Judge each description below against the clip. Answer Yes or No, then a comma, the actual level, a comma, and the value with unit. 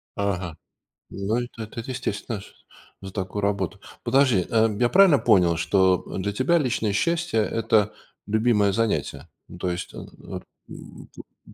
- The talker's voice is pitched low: Yes, low, 105 Hz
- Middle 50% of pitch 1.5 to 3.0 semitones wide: No, average, 3.9 semitones